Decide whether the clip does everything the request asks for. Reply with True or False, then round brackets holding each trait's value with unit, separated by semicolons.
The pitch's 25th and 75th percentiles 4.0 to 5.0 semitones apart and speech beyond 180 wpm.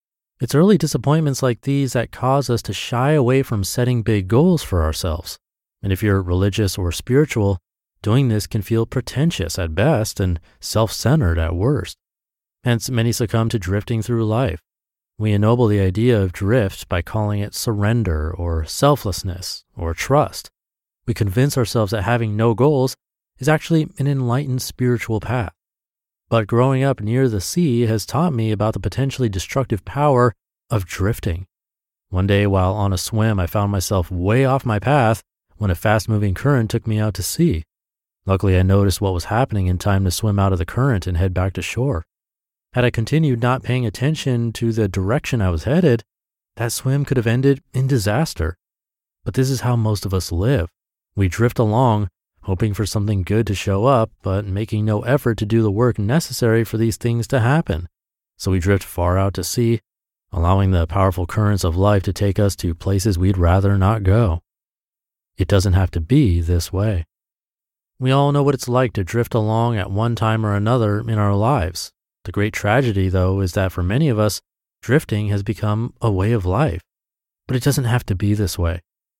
True (4.4 semitones; 190 wpm)